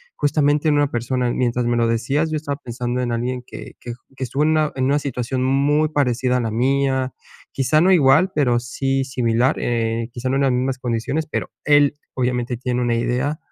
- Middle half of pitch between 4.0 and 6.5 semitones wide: No, average, 2.9 semitones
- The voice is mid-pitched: No, low, 130 Hz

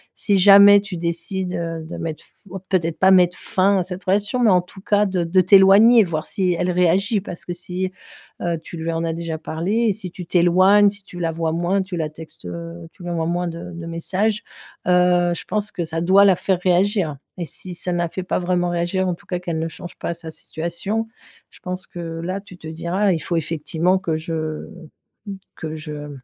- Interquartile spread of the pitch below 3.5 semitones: Yes, narrow, 2.4 semitones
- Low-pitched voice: No, medium, 175 Hz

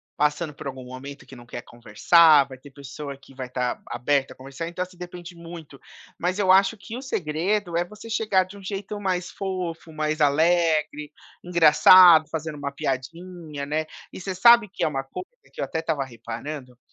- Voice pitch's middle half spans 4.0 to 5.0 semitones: Yes, average, 4.4 semitones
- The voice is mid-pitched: Yes, medium, 160 Hz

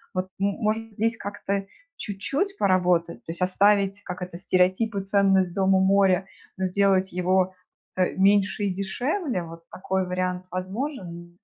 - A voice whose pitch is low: No, high, 190 Hz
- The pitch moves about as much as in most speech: No, narrow, 1.8 semitones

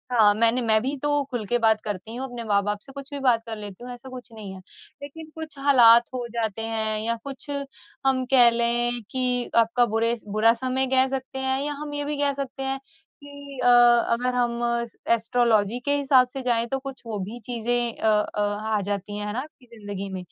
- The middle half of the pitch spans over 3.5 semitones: No, average, 3.2 semitones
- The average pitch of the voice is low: No, high, 240 Hz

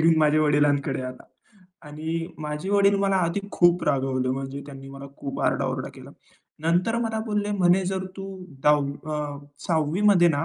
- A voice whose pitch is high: No, medium, 155 Hz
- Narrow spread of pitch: No, average, 4.9 semitones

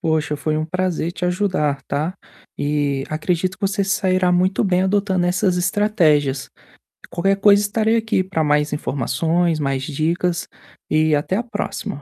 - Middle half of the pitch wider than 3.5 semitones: Yes, average, 3.9 semitones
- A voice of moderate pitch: Yes, medium, 175 Hz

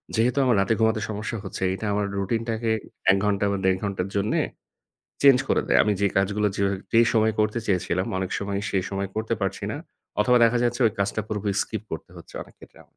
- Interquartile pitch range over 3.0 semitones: No, narrow, 2.4 semitones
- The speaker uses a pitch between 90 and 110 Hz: Yes, low, 105 Hz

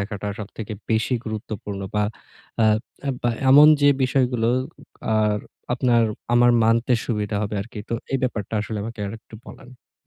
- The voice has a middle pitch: No, low, 110 Hz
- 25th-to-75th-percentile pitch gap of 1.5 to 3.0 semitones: Yes, narrow, 2.5 semitones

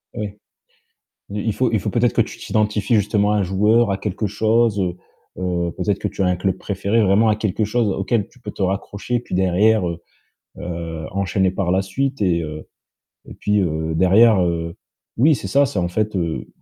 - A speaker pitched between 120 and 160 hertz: No, low, 100 Hz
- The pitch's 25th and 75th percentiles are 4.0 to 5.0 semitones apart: No, average, 3.0 semitones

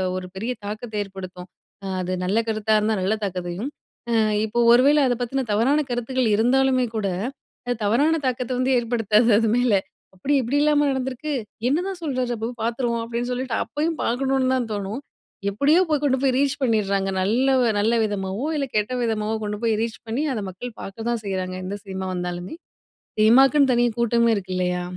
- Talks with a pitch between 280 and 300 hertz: No, high, 235 Hz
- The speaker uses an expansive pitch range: No, average, 4.2 semitones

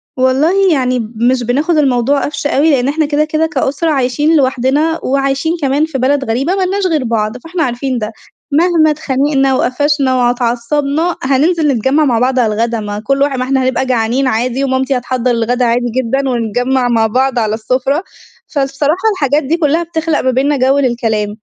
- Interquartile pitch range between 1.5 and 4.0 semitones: Yes, average, 3.2 semitones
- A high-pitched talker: Yes, very high, 265 Hz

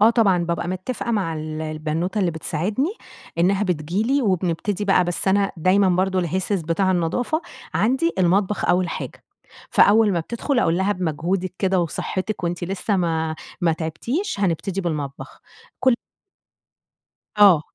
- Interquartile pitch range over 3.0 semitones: Yes, average, 3.4 semitones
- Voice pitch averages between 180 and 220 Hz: Yes, medium, 185 Hz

